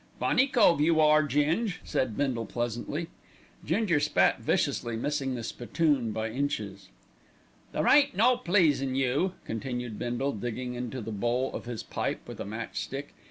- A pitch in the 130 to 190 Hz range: Yes, low, 135 Hz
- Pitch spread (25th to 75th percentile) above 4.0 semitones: Yes, average, 4.7 semitones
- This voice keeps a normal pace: Yes, average, 155 wpm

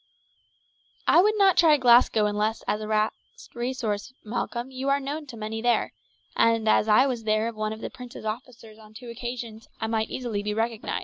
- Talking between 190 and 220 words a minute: Yes, average, 195 wpm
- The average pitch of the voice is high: Yes, high, 230 Hz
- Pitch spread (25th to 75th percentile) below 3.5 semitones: Yes, average, 2.7 semitones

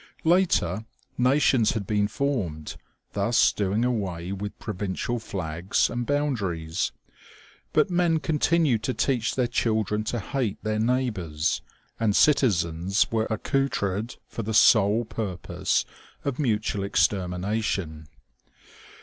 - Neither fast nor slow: No, slow, 115 wpm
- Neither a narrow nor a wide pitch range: Yes, average, 4.6 semitones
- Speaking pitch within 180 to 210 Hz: No, low, 110 Hz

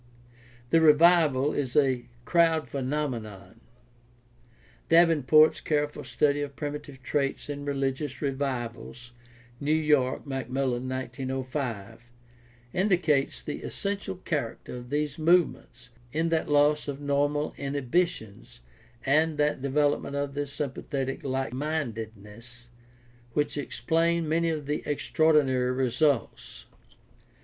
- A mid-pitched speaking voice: Yes, medium, 145 Hz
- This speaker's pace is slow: Yes, slow, 105 wpm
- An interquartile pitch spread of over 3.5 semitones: No, average, 2.8 semitones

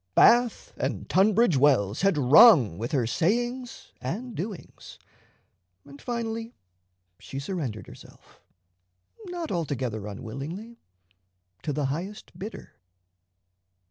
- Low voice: No, medium, 170 Hz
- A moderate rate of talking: No, slow, 100 wpm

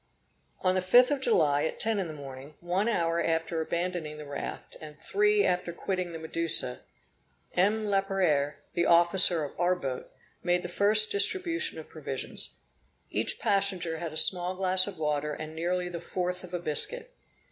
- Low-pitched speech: No, medium, 175 Hz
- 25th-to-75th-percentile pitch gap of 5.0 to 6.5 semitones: No, average, 3.4 semitones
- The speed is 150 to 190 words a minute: Yes, average, 170 wpm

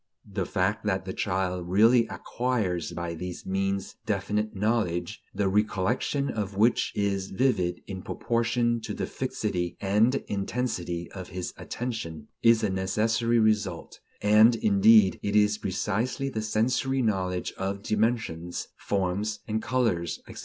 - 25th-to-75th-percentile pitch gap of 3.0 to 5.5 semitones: Yes, average, 3.6 semitones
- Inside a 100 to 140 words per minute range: Yes, slow, 135 wpm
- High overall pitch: No, low, 105 Hz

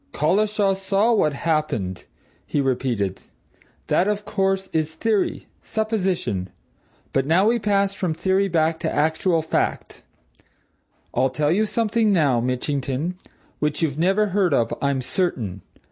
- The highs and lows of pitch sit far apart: Yes, wide, 6.1 semitones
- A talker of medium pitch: Yes, medium, 170 Hz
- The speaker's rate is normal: No, slow, 130 wpm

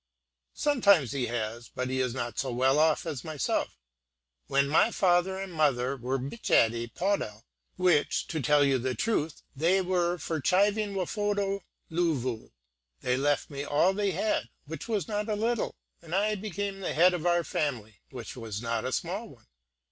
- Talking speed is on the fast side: No, average, 170 wpm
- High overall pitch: No, medium, 160 Hz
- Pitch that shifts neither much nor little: No, wide, 7.0 semitones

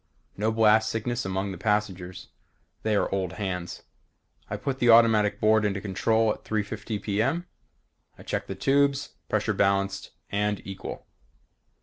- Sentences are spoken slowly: No, average, 145 wpm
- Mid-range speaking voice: No, low, 105 Hz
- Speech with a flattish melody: Yes, narrow, 2.3 semitones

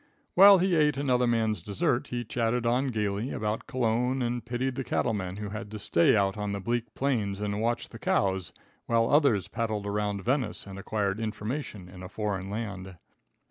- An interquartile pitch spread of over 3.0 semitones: Yes, average, 3.4 semitones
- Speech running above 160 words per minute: Yes, average, 185 wpm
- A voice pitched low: Yes, low, 110 Hz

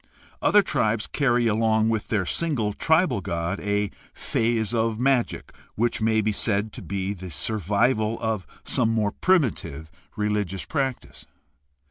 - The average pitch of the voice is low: Yes, low, 110 Hz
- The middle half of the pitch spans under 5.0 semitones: Yes, narrow, 2.5 semitones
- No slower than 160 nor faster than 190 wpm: No, average, 140 wpm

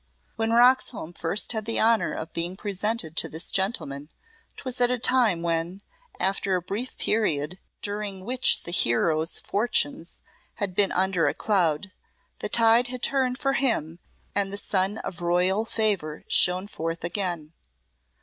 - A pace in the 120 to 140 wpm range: No, average, 150 wpm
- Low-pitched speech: No, high, 195 Hz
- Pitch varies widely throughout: No, average, 4.9 semitones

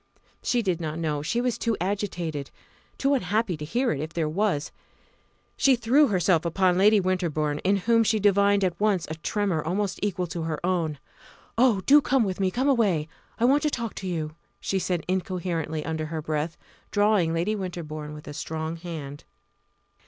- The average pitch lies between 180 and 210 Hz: Yes, medium, 185 Hz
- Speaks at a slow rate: No, average, 180 wpm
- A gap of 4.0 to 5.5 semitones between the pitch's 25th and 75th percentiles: Yes, average, 4.8 semitones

